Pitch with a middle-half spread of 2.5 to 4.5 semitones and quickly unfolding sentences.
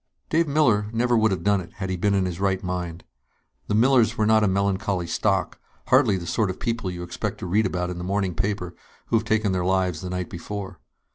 Yes: average, 3.2 semitones; fast, 235 wpm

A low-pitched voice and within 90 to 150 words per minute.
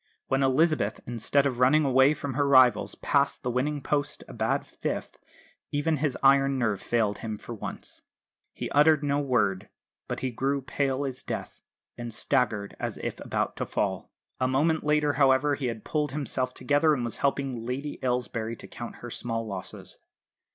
No: low, 130 Hz; average, 175 wpm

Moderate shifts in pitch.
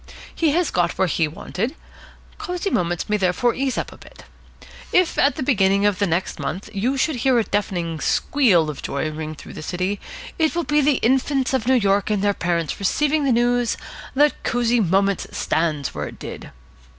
No: wide, 6.9 semitones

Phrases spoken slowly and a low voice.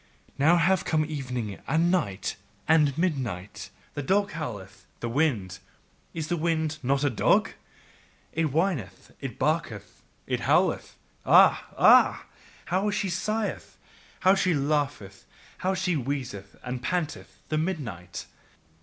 No: slow, 130 wpm; medium, 150 Hz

